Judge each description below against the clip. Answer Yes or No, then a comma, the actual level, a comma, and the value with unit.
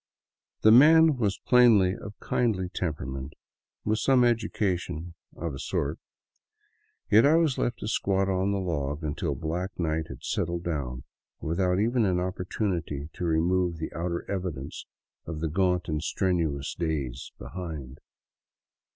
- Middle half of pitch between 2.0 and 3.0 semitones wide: No, average, 4.2 semitones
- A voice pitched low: Yes, very low, 90 Hz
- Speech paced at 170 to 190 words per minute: No, average, 140 wpm